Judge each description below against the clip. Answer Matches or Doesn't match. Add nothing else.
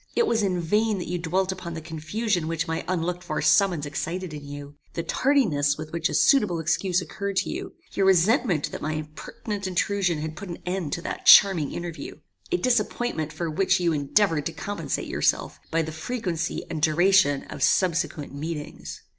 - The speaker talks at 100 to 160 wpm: Doesn't match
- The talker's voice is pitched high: Doesn't match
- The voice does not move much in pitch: Doesn't match